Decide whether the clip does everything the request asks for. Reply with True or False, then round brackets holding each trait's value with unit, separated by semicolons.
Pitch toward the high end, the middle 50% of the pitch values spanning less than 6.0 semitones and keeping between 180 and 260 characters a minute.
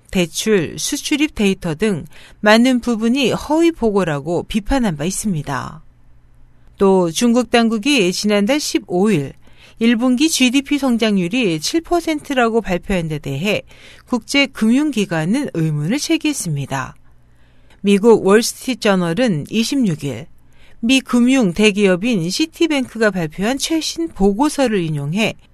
False (215 Hz; 6.6 semitones; 245 characters per minute)